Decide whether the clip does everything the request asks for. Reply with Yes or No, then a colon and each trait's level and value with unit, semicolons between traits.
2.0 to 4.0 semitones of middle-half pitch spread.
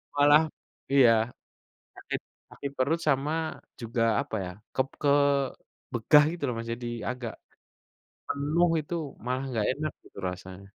No: average, 4.4 semitones